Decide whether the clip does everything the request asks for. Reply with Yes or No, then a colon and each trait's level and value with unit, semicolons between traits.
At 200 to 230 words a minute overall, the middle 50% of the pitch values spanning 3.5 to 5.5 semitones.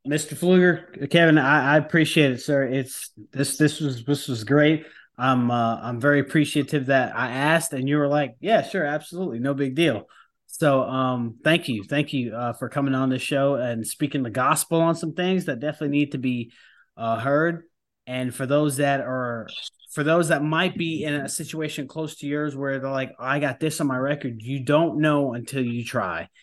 No: fast, 205 wpm; average, 2.9 semitones